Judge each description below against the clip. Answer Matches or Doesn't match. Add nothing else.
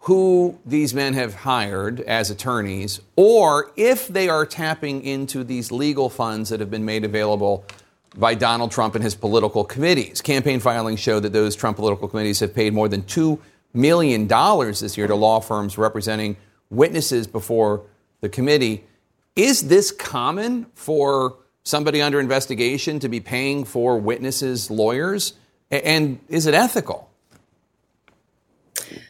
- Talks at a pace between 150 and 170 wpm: Doesn't match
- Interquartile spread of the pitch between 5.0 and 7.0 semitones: Matches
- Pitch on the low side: Matches